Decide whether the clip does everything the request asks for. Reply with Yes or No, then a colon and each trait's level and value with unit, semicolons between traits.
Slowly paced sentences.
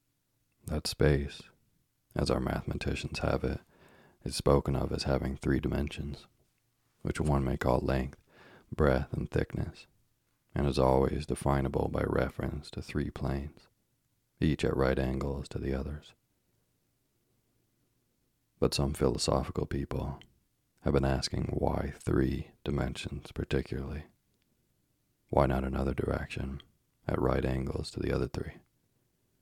Yes: slow, 120 wpm